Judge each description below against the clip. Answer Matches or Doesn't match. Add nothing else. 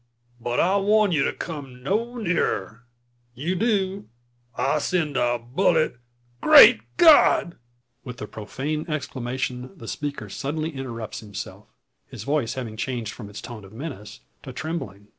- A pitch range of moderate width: Doesn't match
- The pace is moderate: Matches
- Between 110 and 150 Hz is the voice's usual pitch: Matches